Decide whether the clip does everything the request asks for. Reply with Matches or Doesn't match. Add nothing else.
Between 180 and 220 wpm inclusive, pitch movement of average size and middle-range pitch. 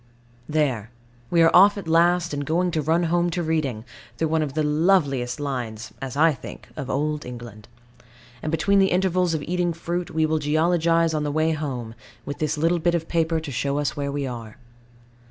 Matches